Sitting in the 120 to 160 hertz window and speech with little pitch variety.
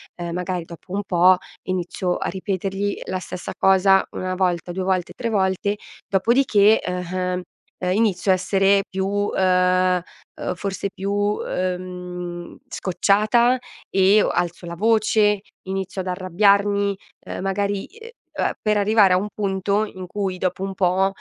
No: high, 190 Hz; narrow, 1.9 semitones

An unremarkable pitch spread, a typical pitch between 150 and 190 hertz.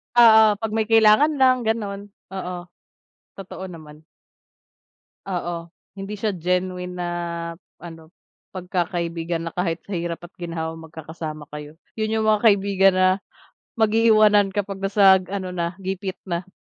Yes: average, 3.5 semitones; medium, 185 Hz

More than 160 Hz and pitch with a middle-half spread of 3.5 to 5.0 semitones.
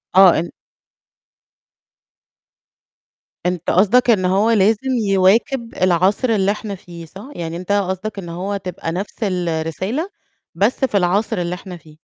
No: high, 190 Hz; average, 3.1 semitones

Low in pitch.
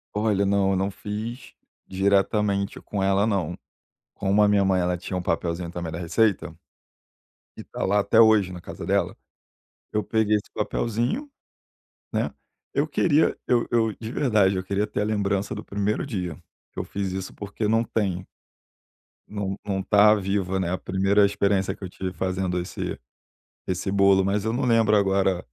Yes: low, 100 Hz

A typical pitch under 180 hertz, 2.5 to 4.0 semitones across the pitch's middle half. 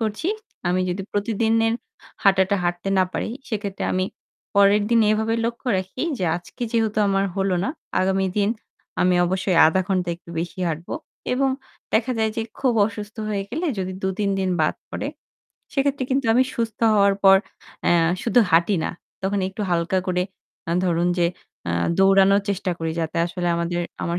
No: high, 195 Hz; average, 3.3 semitones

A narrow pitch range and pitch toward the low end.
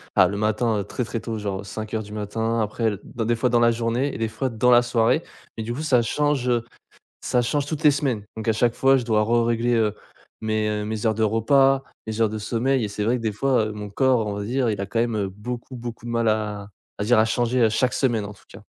Yes: narrow, 2.3 semitones; low, 115 Hz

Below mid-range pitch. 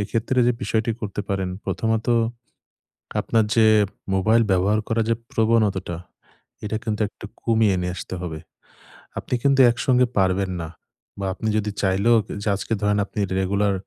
Yes: low, 105 Hz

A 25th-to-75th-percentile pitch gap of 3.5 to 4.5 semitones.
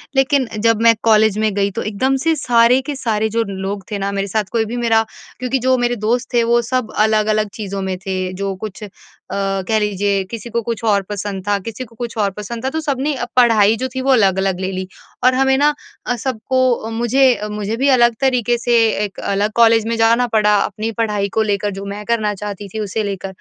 No: average, 3.0 semitones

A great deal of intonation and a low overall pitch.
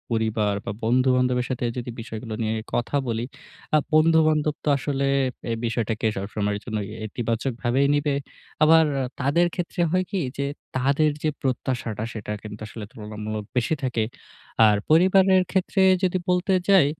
Yes: wide, 5.8 semitones; low, 125 Hz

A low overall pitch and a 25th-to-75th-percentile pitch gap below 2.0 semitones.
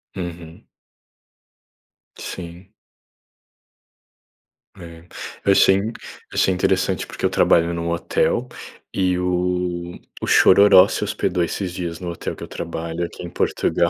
Yes: very low, 90 Hz; narrow, 1.4 semitones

